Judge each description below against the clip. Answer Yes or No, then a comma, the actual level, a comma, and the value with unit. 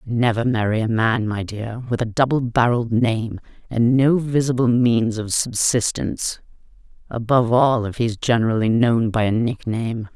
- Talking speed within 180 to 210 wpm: No, average, 155 wpm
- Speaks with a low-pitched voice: Yes, low, 115 Hz